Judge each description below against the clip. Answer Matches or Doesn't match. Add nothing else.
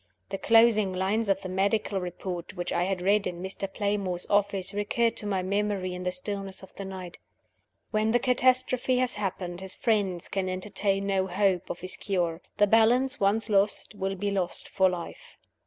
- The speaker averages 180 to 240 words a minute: Matches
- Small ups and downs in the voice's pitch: Matches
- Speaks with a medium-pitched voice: Doesn't match